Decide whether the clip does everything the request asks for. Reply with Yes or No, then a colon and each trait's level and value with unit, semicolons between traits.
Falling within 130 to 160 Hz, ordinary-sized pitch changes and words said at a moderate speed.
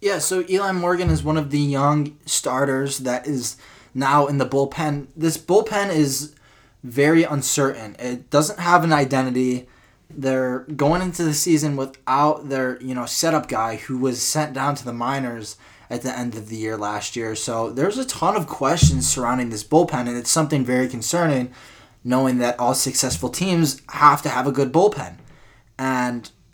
Yes: low, 135 Hz; average, 3.4 semitones; average, 175 wpm